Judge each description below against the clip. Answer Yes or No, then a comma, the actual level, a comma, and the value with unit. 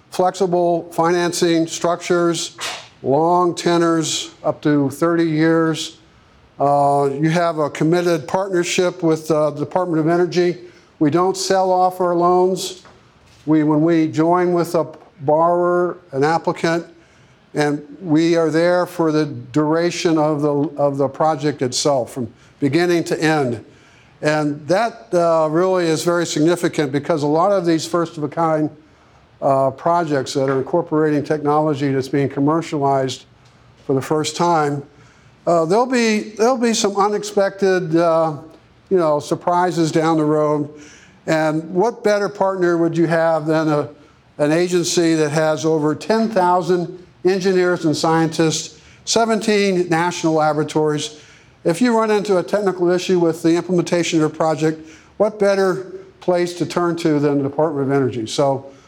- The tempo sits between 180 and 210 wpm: No, average, 145 wpm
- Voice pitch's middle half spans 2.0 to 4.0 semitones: Yes, average, 2.8 semitones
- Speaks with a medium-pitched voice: Yes, medium, 165 Hz